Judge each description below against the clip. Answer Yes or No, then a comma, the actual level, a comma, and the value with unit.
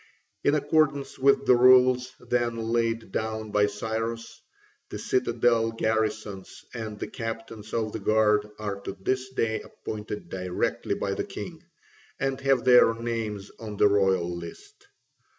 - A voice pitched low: Yes, low, 115 Hz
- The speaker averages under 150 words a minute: Yes, average, 140 wpm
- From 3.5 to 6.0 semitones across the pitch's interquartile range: No, average, 2.7 semitones